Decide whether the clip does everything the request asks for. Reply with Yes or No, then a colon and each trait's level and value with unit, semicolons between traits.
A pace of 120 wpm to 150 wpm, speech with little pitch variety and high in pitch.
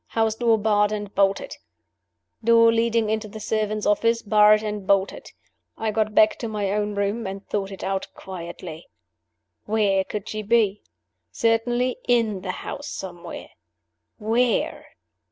Yes: average, 140 wpm; narrow, 2.2 semitones; high, 215 Hz